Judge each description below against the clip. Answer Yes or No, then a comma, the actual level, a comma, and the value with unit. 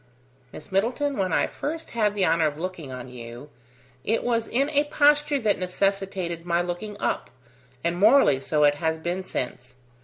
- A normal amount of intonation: No, wide, 6.0 semitones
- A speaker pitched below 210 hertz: Yes, medium, 185 Hz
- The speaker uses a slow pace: No, average, 175 wpm